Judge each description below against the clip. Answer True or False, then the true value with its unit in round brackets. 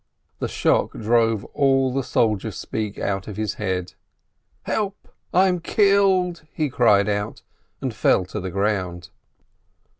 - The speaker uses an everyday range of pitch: False (7.2 semitones)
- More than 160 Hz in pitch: False (110 Hz)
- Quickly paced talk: False (140 wpm)